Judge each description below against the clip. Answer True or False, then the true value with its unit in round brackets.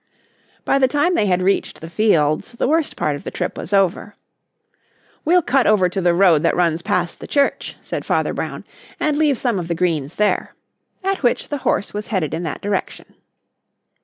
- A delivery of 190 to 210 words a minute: True (195 wpm)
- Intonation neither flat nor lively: False (7.5 semitones)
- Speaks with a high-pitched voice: True (195 Hz)